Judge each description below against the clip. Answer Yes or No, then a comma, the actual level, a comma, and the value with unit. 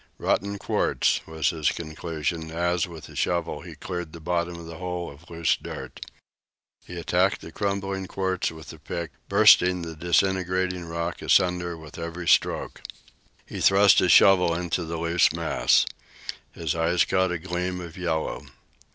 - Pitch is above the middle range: No, very low, 85 Hz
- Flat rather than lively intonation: Yes, narrow, 1.7 semitones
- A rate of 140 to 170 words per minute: Yes, average, 160 wpm